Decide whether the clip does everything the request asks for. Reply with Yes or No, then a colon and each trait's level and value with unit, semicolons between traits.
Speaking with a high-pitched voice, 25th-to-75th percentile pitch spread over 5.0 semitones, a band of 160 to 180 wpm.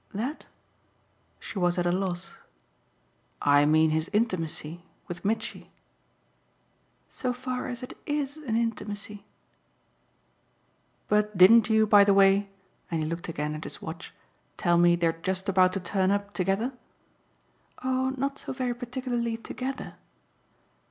No: high, 200 Hz; wide, 5.4 semitones; slow, 135 wpm